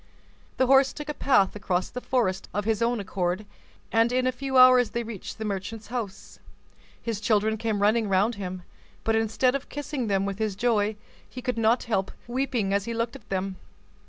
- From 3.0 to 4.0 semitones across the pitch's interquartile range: Yes, average, 3.6 semitones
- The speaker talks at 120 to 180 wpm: No, average, 190 wpm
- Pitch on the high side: Yes, high, 225 Hz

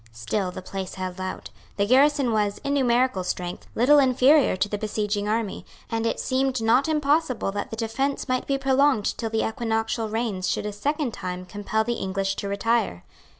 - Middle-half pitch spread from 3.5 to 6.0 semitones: Yes, average, 4.5 semitones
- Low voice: No, high, 225 Hz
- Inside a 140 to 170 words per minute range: No, average, 185 wpm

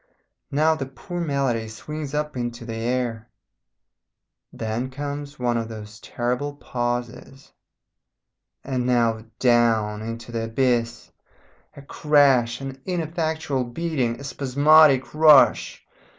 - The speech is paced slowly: Yes, slow, 110 wpm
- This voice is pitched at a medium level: No, low, 130 Hz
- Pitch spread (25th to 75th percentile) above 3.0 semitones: Yes, average, 3.6 semitones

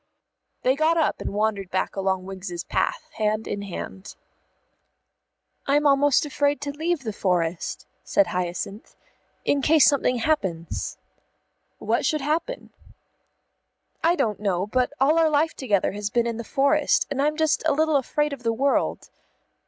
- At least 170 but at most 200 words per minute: No, average, 155 wpm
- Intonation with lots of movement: Yes, wide, 6.8 semitones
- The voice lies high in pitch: Yes, very high, 255 Hz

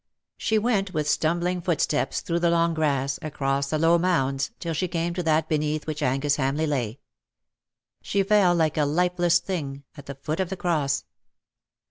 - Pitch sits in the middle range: Yes, medium, 160 Hz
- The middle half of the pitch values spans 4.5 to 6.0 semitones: No, average, 3.6 semitones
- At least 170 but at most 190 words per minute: Yes, average, 175 wpm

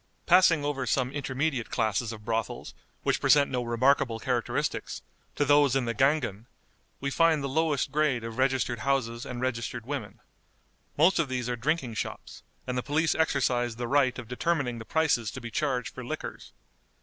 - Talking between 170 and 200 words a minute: Yes, average, 175 wpm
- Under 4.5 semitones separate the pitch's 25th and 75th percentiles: Yes, average, 3.6 semitones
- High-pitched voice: No, low, 130 Hz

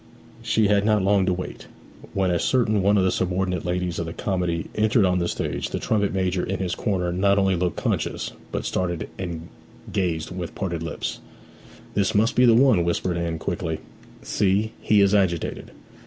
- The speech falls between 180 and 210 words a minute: Yes, average, 185 wpm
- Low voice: Yes, very low, 95 Hz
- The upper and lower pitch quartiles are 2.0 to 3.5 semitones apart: Yes, narrow, 2.6 semitones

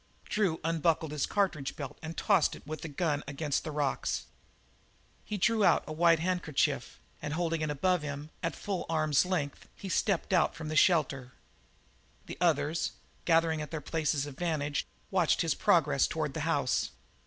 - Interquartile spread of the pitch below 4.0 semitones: Yes, narrow, 2.5 semitones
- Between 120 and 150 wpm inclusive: No, average, 175 wpm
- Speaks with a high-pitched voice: No, medium, 160 Hz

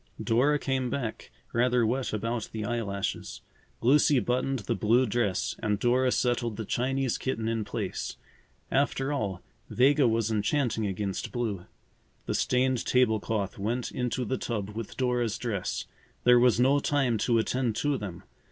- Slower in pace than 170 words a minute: Yes, average, 150 wpm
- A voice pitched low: Yes, low, 120 Hz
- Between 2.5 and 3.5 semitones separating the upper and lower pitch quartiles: Yes, average, 3.0 semitones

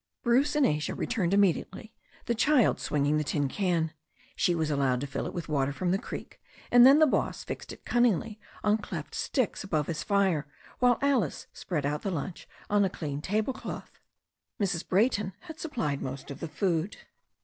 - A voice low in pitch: No, medium, 185 Hz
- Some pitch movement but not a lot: No, wide, 6.9 semitones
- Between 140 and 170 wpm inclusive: No, average, 185 wpm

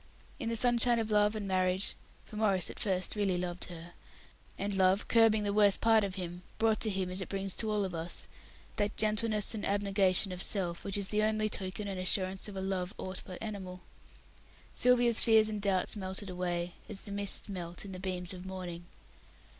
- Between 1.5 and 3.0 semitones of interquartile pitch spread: Yes, narrow, 2.5 semitones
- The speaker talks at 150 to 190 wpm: No, average, 200 wpm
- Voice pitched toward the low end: No, high, 195 Hz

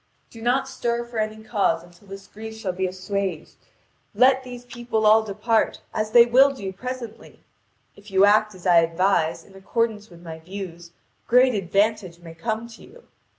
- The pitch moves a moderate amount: Yes, average, 3.9 semitones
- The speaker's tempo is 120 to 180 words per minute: Yes, average, 175 wpm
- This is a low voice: No, high, 210 Hz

